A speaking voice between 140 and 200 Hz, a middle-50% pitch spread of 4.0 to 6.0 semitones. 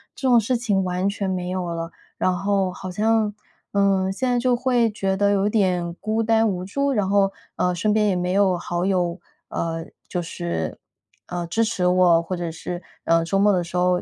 No: high, 190 Hz; average, 2.9 semitones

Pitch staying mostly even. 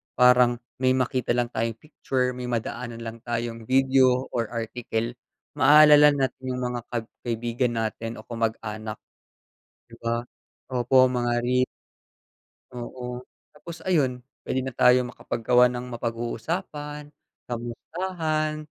Yes: narrow, 2.0 semitones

